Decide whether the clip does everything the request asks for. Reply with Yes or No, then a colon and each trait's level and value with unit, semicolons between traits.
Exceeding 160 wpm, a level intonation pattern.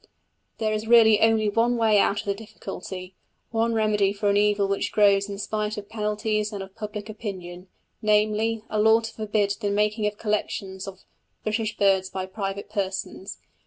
Yes: average, 175 wpm; narrow, 1.6 semitones